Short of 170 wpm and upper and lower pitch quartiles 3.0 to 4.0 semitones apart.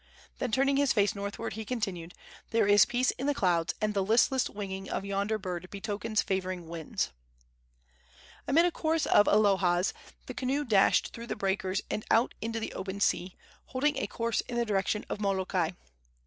No: average, 175 wpm; average, 3.5 semitones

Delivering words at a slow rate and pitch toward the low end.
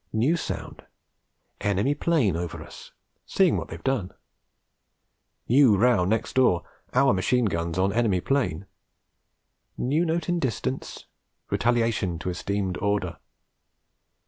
Yes: slow, 120 wpm; low, 110 Hz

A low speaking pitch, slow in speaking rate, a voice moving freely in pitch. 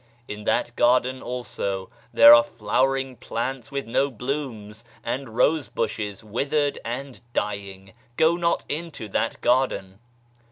No: low, 120 Hz; slow, 125 wpm; average, 4.3 semitones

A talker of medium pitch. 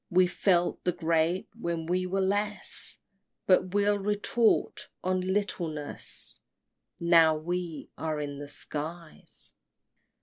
Yes: medium, 175 Hz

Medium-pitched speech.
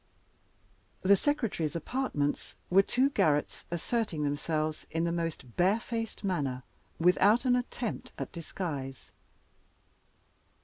Yes: medium, 175 Hz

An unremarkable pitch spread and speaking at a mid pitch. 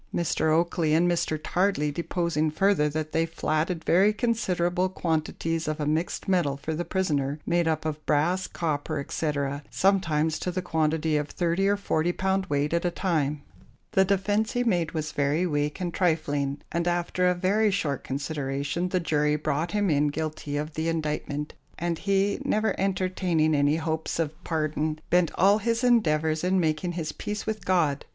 Yes: average, 3.2 semitones; medium, 165 Hz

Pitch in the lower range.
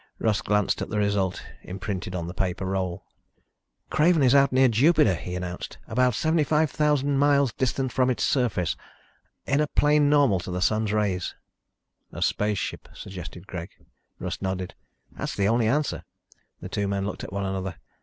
Yes: low, 105 Hz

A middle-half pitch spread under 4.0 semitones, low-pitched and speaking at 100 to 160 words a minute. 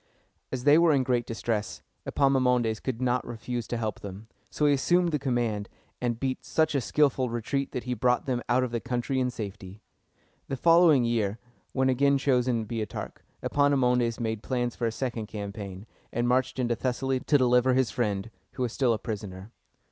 No: average, 2.8 semitones; low, 125 Hz; average, 185 wpm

